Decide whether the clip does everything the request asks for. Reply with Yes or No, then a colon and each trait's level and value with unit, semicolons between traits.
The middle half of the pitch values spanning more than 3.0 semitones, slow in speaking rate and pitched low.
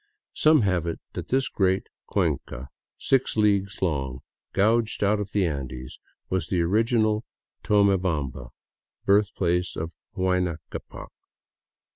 Yes: average, 4.0 semitones; slow, 120 wpm; very low, 95 Hz